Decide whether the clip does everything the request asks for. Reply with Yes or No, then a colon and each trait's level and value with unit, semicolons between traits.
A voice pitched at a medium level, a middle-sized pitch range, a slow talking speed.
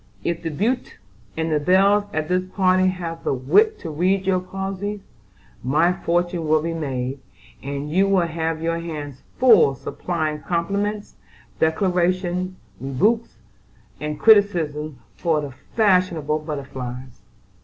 Yes: medium, 170 Hz; average, 3.8 semitones; slow, 125 wpm